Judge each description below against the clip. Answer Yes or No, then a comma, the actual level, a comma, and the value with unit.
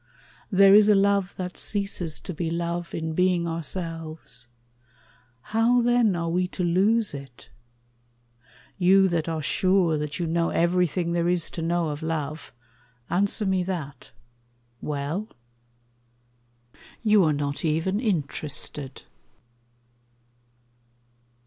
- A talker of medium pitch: Yes, medium, 170 Hz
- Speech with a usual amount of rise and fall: Yes, average, 3.3 semitones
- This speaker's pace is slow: Yes, slow, 115 wpm